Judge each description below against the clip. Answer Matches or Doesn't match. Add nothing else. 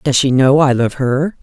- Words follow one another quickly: Matches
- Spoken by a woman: Matches